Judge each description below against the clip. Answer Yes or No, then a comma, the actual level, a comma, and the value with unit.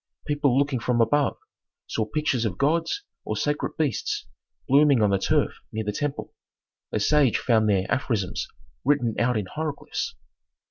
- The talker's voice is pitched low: Yes, low, 130 Hz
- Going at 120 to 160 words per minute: Yes, average, 150 wpm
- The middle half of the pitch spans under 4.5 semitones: No, average, 5.1 semitones